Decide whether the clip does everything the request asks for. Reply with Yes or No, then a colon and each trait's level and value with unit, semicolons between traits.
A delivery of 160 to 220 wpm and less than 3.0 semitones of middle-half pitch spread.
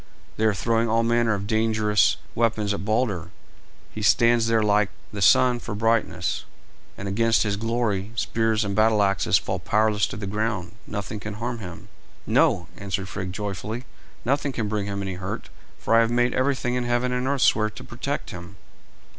Yes: average, 180 wpm; narrow, 2.4 semitones